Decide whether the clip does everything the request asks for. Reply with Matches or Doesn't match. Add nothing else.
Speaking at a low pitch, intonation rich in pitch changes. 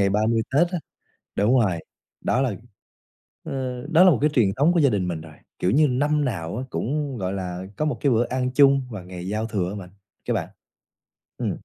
Matches